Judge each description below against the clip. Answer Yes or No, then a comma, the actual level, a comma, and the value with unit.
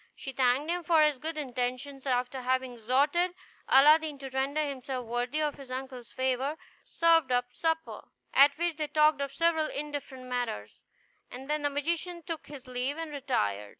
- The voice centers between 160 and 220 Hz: No, very high, 280 Hz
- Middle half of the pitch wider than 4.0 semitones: No, average, 3.3 semitones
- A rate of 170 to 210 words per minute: Yes, average, 175 wpm